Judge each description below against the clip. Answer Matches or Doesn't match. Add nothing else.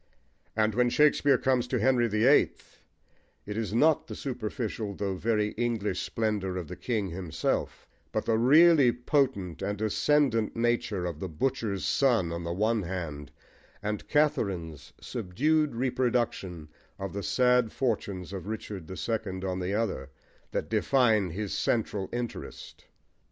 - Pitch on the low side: Matches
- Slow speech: Doesn't match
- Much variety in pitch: Doesn't match